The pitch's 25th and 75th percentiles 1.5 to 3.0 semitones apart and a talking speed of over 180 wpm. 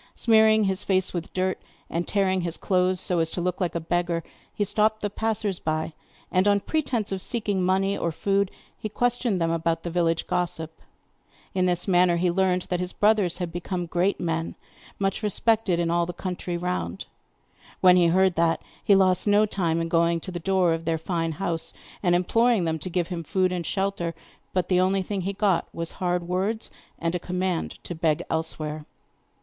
Yes: narrow, 2.5 semitones; average, 195 wpm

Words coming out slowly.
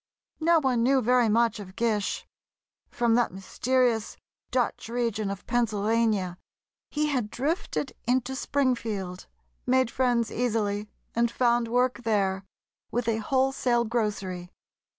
Yes: slow, 120 wpm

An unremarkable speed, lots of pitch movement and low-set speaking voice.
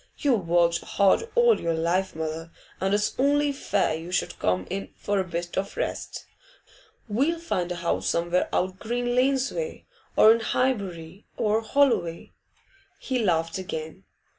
No: average, 155 wpm; wide, 6.7 semitones; high, 190 Hz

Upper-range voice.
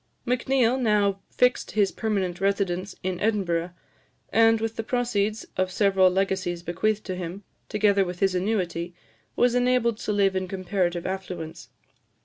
Yes: high, 195 Hz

